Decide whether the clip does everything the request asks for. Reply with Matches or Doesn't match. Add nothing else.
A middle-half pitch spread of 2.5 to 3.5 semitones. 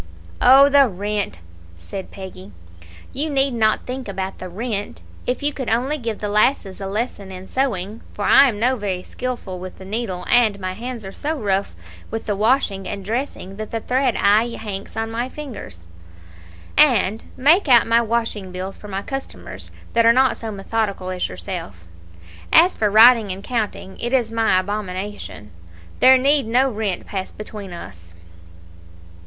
Doesn't match